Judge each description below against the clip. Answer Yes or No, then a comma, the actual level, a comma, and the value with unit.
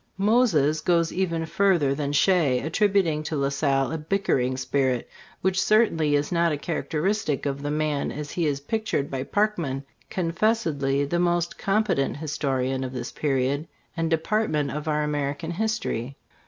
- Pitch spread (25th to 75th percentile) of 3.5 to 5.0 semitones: Yes, average, 4.2 semitones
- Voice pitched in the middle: Yes, medium, 155 Hz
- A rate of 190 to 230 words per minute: No, average, 155 wpm